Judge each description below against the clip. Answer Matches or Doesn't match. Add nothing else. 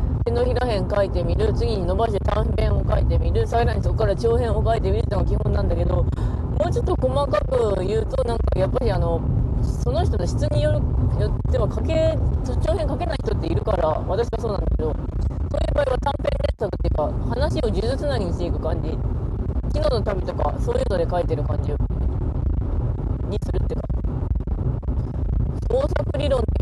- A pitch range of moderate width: Matches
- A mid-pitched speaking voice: Doesn't match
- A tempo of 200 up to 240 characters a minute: Doesn't match